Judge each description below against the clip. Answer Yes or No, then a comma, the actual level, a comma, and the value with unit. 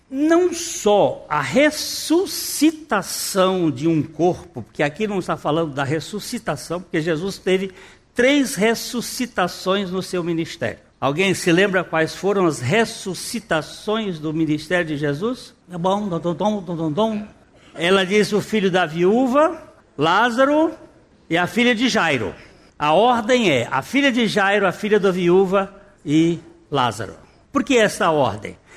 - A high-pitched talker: Yes, high, 195 Hz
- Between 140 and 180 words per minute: No, average, 130 wpm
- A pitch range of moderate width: No, wide, 5.9 semitones